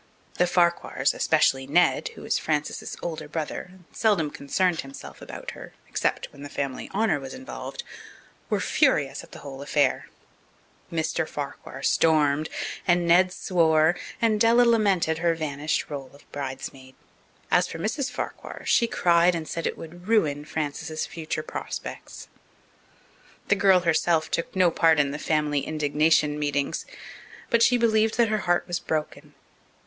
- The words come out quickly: No, average, 150 wpm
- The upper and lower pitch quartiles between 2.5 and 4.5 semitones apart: Yes, average, 4.0 semitones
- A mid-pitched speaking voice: Yes, medium, 165 Hz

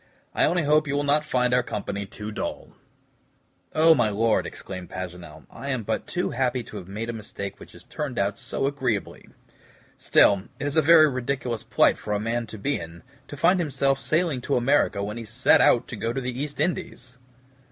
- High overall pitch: No, low, 125 Hz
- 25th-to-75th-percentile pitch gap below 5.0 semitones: No, average, 5.3 semitones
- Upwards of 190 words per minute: Yes, fast, 205 wpm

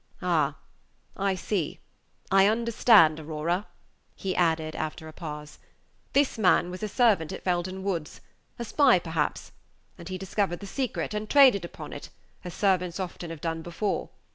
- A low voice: No, medium, 185 Hz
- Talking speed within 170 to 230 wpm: No, average, 155 wpm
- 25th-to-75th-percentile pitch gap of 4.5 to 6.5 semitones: No, average, 4.0 semitones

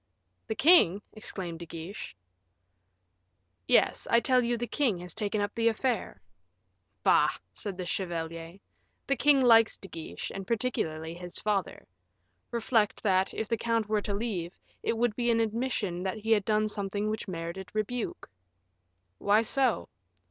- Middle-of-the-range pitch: No, high, 210 Hz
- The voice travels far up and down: No, average, 3.8 semitones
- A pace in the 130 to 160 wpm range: Yes, average, 155 wpm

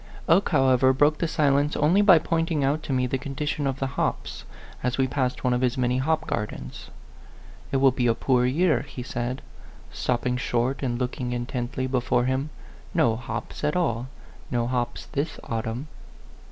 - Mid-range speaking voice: No, low, 130 Hz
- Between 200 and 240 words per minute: No, average, 180 wpm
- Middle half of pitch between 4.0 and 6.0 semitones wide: No, average, 2.8 semitones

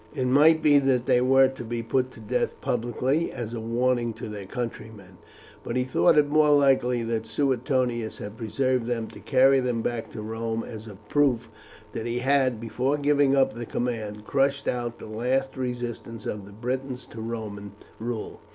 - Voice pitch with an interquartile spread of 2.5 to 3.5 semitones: Yes, average, 2.9 semitones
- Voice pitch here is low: Yes, low, 120 Hz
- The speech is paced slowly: No, average, 185 wpm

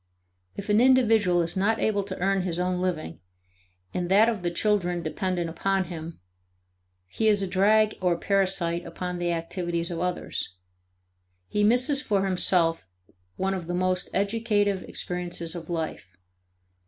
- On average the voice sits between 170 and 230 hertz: Yes, medium, 185 Hz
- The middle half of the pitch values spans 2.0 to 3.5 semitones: Yes, average, 2.8 semitones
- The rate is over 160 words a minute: No, average, 150 wpm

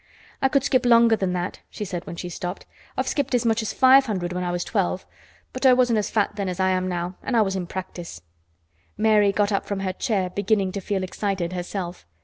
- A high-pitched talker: Yes, high, 195 Hz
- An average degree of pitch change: Yes, average, 3.5 semitones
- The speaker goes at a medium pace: No, fast, 235 wpm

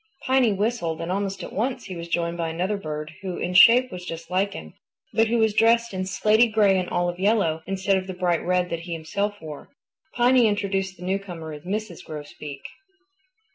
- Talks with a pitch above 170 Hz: Yes, high, 190 Hz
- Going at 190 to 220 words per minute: Yes, average, 200 wpm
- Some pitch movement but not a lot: Yes, average, 3.9 semitones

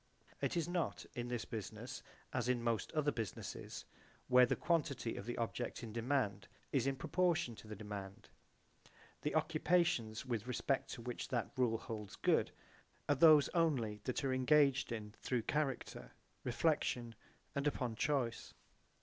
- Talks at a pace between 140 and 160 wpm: Yes, average, 150 wpm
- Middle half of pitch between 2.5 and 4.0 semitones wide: No, average, 4.5 semitones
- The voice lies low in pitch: Yes, low, 125 Hz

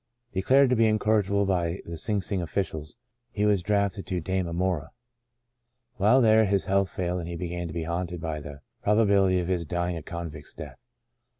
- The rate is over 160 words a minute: Yes, average, 185 wpm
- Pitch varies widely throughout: No, average, 3.1 semitones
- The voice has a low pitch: Yes, very low, 95 Hz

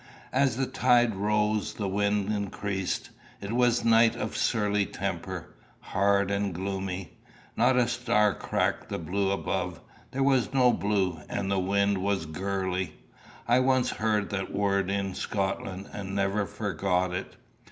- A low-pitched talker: Yes, low, 100 Hz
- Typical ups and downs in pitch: No, narrow, 2.2 semitones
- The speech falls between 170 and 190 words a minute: No, average, 150 wpm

